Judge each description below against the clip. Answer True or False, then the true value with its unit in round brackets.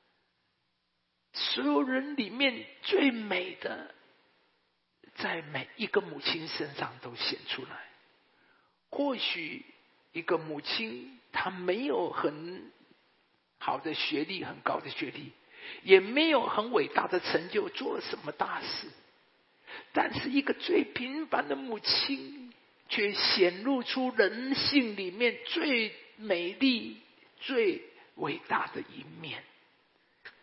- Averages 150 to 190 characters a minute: True (160 characters per minute)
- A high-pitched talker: True (260 Hz)